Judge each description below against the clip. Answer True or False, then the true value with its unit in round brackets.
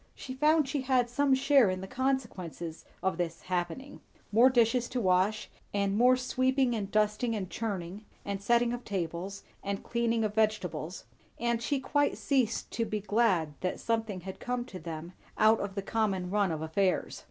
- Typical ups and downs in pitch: True (4.6 semitones)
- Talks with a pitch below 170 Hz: False (215 Hz)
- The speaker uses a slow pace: False (175 wpm)